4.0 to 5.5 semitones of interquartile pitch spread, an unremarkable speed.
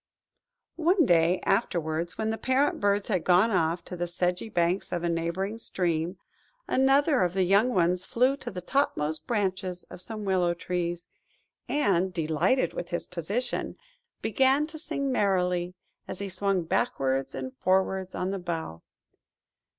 Yes: average, 4.4 semitones; average, 150 wpm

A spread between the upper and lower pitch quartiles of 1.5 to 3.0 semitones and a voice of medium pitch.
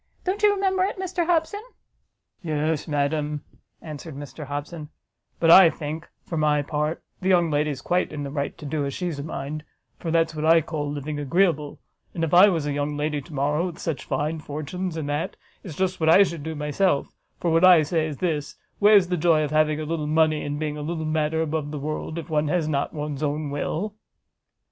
Yes: narrow, 2.5 semitones; medium, 155 Hz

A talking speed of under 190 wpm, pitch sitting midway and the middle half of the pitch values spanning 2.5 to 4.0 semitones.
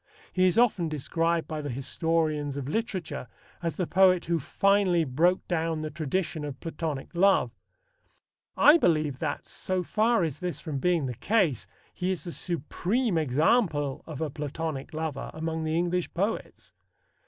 Yes: average, 155 wpm; medium, 165 Hz; average, 3.4 semitones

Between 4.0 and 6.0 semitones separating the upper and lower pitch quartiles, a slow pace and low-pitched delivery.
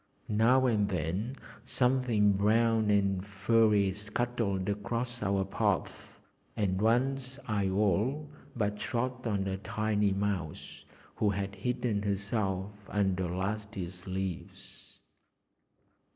No: average, 3.1 semitones; slow, 110 wpm; low, 105 Hz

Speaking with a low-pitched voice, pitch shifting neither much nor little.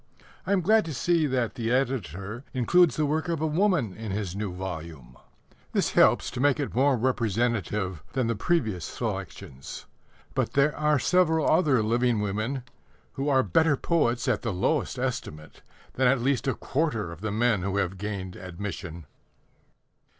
No: low, 120 Hz; wide, 6.6 semitones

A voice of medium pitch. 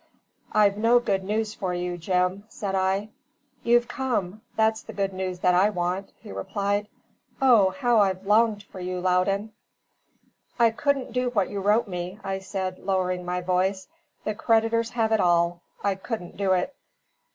No: high, 195 Hz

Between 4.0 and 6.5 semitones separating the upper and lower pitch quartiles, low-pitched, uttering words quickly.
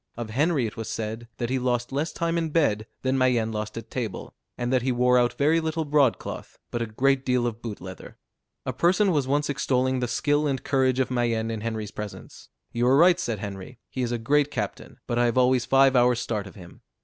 No: average, 3.2 semitones; low, 125 Hz; fast, 230 wpm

